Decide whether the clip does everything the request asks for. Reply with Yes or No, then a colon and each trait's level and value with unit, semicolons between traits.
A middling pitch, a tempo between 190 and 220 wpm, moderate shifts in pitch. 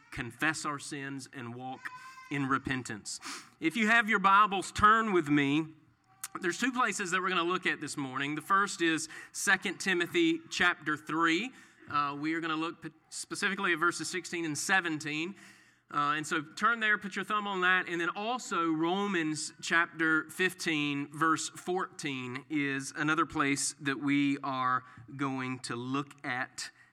No: medium, 160 Hz; average, 165 wpm; average, 4.3 semitones